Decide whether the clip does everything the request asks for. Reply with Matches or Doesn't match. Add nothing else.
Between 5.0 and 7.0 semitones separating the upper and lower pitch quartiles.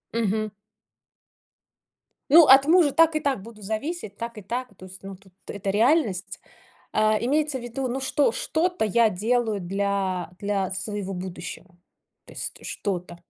Matches